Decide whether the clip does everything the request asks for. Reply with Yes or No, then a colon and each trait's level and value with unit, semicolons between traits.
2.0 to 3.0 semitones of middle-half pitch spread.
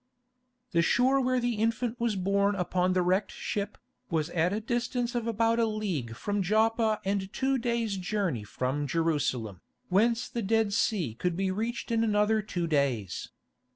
No: average, 4.5 semitones